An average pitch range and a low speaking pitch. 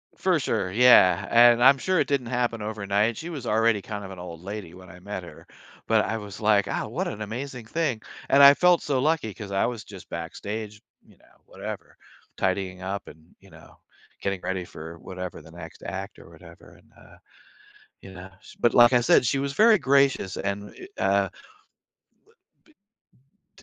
Yes: average, 4.8 semitones; low, 105 Hz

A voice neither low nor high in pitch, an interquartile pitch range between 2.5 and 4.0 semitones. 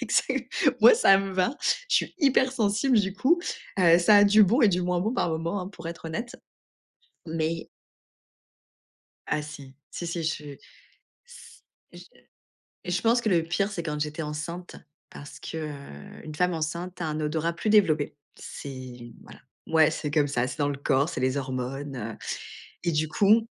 No: medium, 165 Hz; average, 4.8 semitones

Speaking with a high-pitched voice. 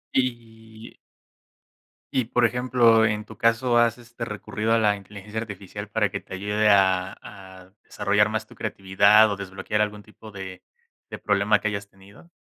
No: low, 105 Hz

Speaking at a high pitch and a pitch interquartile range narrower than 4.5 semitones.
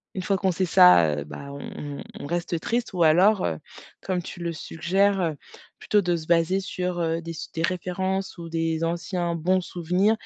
No: medium, 175 Hz; narrow, 2.4 semitones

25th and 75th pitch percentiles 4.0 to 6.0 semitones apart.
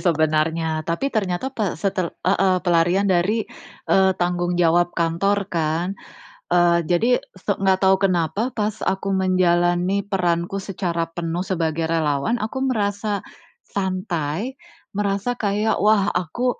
No: average, 2.9 semitones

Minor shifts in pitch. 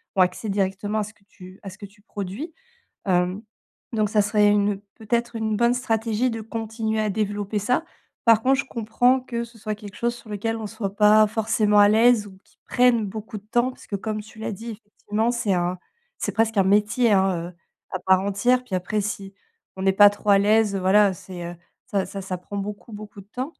Yes: narrow, 2.2 semitones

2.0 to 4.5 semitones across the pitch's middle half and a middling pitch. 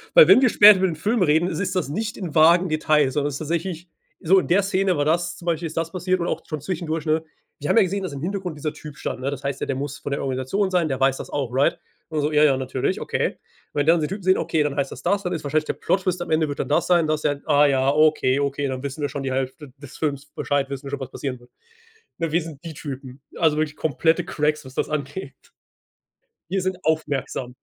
Yes: average, 3.7 semitones; medium, 155 Hz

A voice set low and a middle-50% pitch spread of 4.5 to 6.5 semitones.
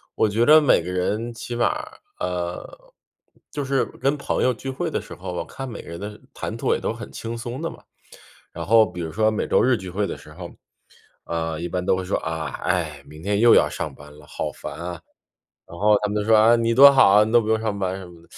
Yes: low, 105 Hz; average, 5.0 semitones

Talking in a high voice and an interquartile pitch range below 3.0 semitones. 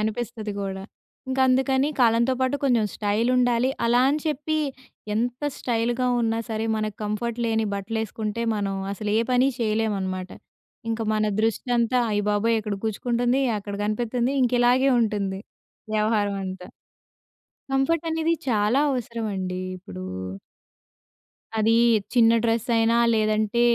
Yes: high, 225 Hz; narrow, 2.6 semitones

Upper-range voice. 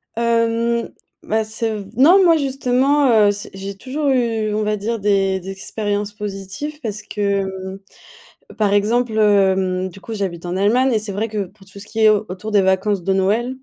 Yes: high, 210 Hz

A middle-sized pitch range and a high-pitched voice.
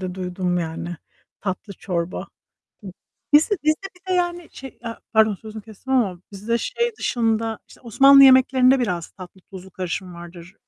No: wide, 6.3 semitones; high, 215 Hz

